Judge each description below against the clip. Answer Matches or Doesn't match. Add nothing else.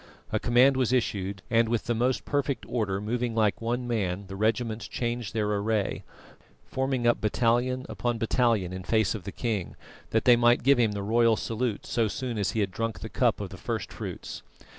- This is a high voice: Doesn't match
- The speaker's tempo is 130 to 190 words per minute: Doesn't match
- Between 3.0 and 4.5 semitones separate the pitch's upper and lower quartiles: Doesn't match